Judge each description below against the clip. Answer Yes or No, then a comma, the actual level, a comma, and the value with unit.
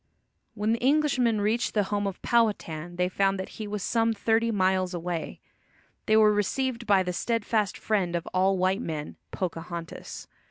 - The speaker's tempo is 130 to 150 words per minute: No, average, 165 wpm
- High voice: Yes, high, 205 Hz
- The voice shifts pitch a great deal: No, average, 3.7 semitones